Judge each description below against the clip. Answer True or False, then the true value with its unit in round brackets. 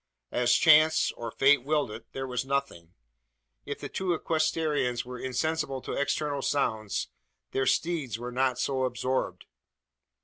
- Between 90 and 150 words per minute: True (140 wpm)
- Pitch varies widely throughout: False (3.4 semitones)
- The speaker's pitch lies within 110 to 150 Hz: True (135 Hz)